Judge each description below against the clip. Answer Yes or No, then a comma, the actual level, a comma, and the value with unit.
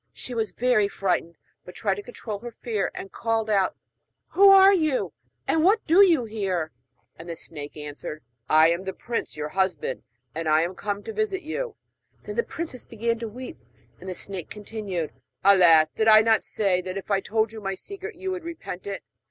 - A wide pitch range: Yes, wide, 5.7 semitones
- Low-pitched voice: No, high, 210 Hz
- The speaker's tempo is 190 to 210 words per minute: Yes, average, 200 wpm